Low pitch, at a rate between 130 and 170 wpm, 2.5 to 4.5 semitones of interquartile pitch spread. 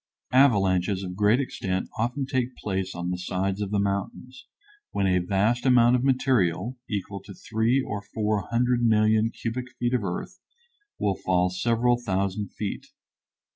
Yes: low, 105 Hz; average, 155 wpm; average, 4.2 semitones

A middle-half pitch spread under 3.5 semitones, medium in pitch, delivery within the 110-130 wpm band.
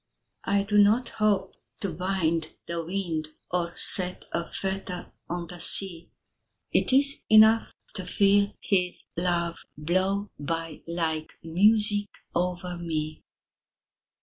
Yes: average, 3.0 semitones; medium, 180 Hz; slow, 120 wpm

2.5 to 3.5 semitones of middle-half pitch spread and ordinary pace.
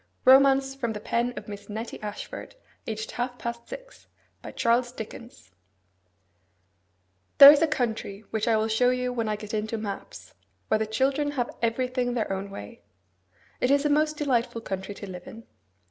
No: average, 4.4 semitones; average, 145 wpm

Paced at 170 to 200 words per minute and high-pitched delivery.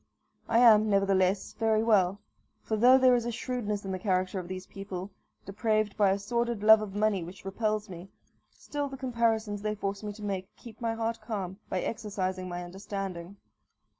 Yes: average, 185 wpm; high, 205 Hz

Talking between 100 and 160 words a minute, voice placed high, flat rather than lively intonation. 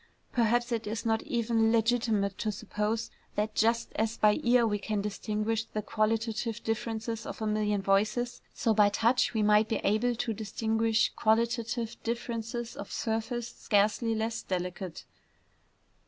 Yes: average, 150 wpm; high, 225 Hz; narrow, 1.5 semitones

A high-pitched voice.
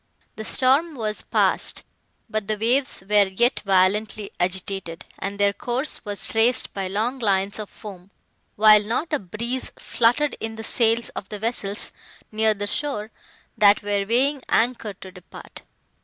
Yes: high, 215 Hz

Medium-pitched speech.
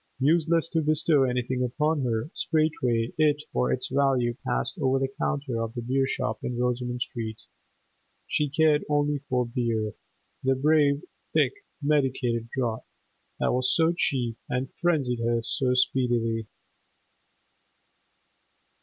No: low, 130 Hz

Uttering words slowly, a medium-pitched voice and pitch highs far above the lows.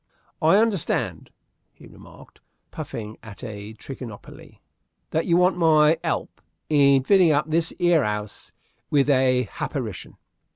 Yes: slow, 125 wpm; medium, 145 Hz; wide, 5.9 semitones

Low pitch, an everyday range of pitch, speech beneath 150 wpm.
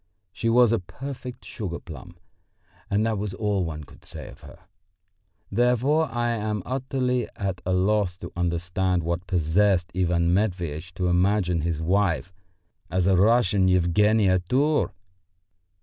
Yes: very low, 95 Hz; average, 4.2 semitones; average, 140 wpm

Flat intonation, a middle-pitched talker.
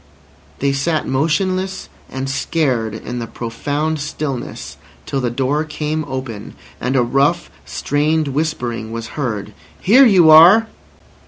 No: average, 4.2 semitones; medium, 145 Hz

